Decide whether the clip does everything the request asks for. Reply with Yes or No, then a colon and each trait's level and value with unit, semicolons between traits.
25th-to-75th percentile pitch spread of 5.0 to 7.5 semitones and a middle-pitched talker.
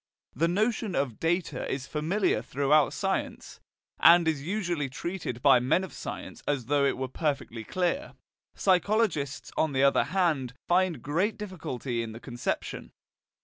Yes: wide, 5.5 semitones; medium, 150 Hz